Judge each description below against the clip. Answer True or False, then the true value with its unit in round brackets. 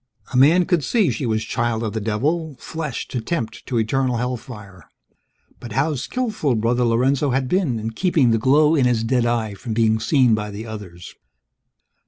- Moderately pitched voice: False (120 Hz)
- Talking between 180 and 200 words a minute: True (185 wpm)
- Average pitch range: True (4.1 semitones)